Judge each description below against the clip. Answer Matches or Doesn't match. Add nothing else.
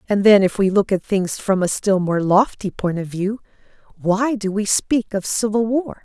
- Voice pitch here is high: Matches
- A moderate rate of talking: Doesn't match